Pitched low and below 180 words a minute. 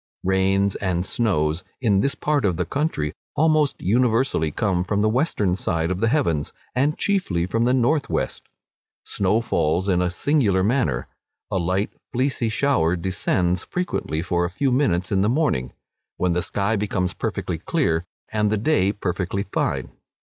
Yes: low, 100 Hz; average, 165 wpm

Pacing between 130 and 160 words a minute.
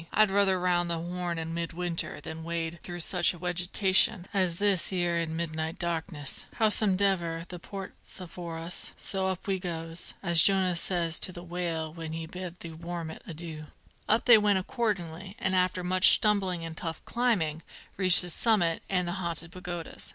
No: average, 175 wpm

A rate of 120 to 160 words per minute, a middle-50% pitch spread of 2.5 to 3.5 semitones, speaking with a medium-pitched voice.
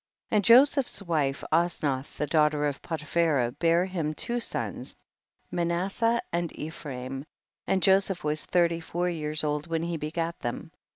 Yes: average, 150 wpm; average, 2.9 semitones; medium, 165 Hz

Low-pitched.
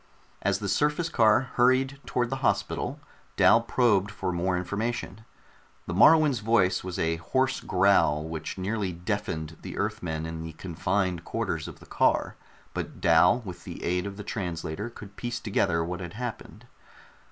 Yes: very low, 95 Hz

